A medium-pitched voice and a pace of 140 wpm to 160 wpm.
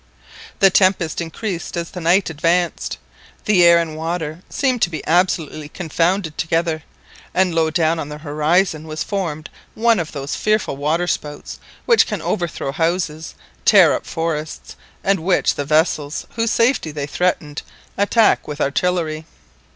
Yes: medium, 165 Hz; average, 145 wpm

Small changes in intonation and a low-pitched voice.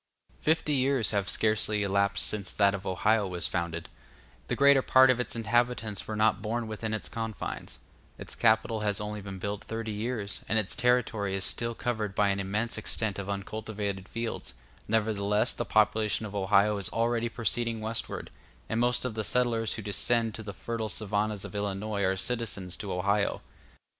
Yes: narrow, 2.3 semitones; low, 110 Hz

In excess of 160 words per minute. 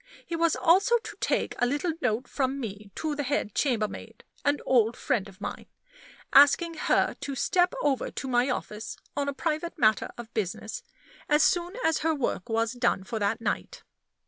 Yes: average, 180 wpm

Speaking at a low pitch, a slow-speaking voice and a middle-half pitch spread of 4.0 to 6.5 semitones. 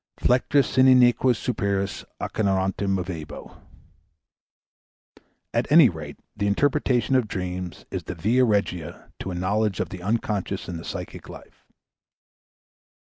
Yes: low, 100 Hz; slow, 125 wpm; average, 5.1 semitones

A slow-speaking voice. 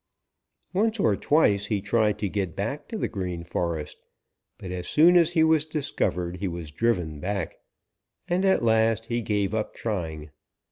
No: average, 170 wpm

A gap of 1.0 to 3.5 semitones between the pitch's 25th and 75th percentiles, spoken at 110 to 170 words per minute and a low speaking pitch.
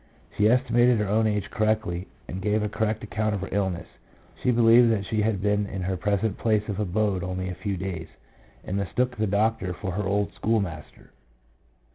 No: narrow, 2.6 semitones; average, 190 wpm; low, 105 Hz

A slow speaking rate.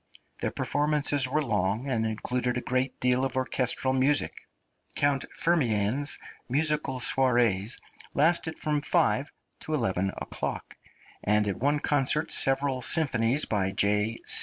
Yes: slow, 125 wpm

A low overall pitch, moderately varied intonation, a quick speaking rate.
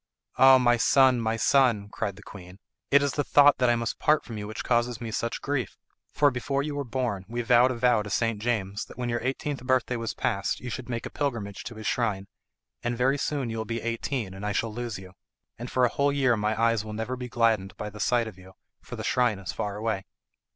Yes: low, 115 Hz; average, 3.1 semitones; fast, 245 wpm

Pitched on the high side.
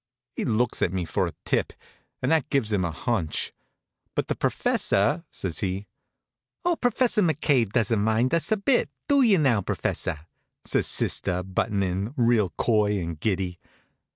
No: low, 110 Hz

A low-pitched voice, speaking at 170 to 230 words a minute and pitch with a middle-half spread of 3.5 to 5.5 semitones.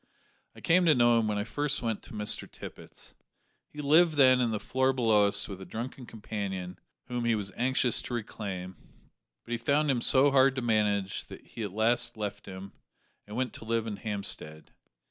Yes: low, 115 Hz; average, 200 wpm; average, 4.0 semitones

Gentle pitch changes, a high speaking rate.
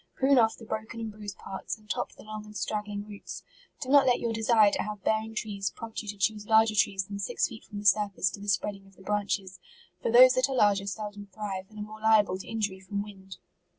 Yes: narrow, 1.7 semitones; fast, 250 wpm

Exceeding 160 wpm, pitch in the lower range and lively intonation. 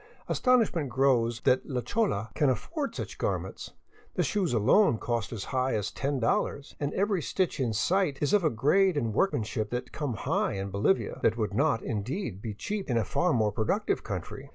Yes: average, 185 wpm; low, 130 Hz; wide, 8.1 semitones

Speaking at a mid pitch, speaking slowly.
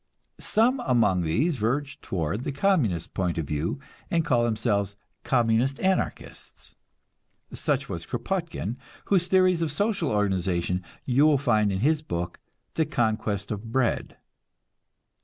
No: low, 120 Hz; slow, 130 wpm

